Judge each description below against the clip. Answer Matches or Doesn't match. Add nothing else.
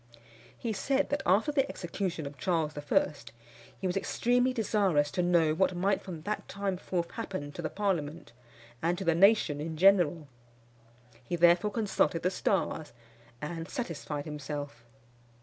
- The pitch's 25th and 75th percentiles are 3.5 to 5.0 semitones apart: Matches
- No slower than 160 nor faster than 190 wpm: Doesn't match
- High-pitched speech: Doesn't match